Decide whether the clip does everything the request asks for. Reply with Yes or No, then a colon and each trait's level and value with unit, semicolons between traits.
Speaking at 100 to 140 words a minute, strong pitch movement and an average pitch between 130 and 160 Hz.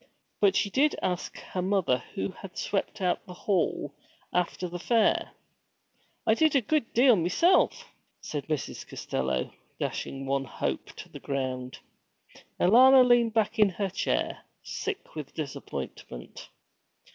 No: slow, 135 wpm; wide, 7.6 semitones; high, 190 Hz